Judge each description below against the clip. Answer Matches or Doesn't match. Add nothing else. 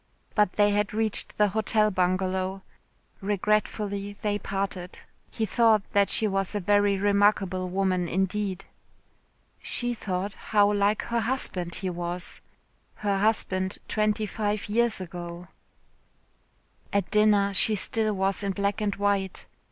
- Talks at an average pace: Doesn't match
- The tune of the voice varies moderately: Doesn't match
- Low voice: Doesn't match